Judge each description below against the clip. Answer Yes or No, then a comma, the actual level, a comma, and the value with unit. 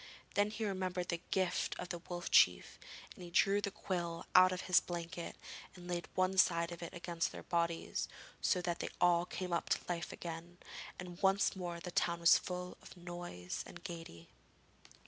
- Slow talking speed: No, average, 185 wpm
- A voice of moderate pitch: Yes, medium, 175 Hz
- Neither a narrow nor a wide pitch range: No, narrow, 1.3 semitones